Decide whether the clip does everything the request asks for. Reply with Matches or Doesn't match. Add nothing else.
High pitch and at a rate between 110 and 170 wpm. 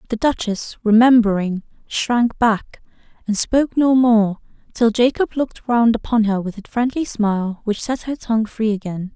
Matches